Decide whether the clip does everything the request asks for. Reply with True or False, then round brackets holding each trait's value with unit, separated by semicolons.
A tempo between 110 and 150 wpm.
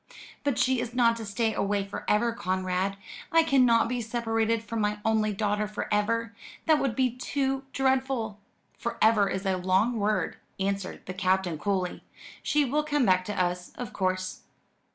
False (175 wpm)